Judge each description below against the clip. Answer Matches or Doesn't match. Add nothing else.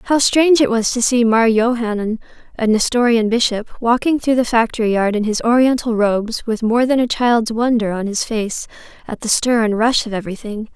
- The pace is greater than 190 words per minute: Matches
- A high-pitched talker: Matches